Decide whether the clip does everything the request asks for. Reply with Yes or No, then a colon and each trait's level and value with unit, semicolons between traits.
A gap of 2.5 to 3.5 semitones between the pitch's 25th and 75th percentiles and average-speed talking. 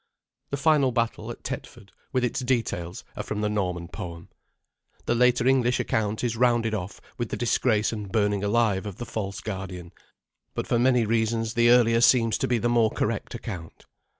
Yes: average, 2.8 semitones; average, 180 wpm